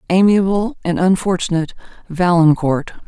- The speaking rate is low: Yes, slow, 80 wpm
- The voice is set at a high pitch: No, medium, 180 Hz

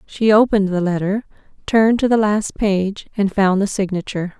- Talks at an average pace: Yes, average, 175 wpm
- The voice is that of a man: No, female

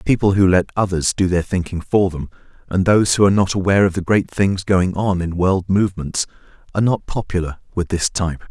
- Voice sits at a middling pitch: No, very low, 95 Hz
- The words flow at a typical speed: No, fast, 210 wpm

